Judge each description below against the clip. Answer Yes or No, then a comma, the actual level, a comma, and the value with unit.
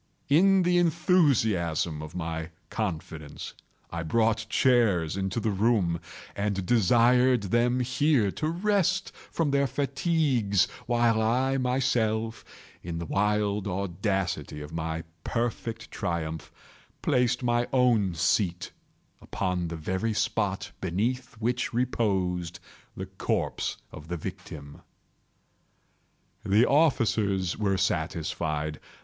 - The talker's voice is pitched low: Yes, low, 105 Hz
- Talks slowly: Yes, slow, 105 wpm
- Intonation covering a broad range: Yes, wide, 6.0 semitones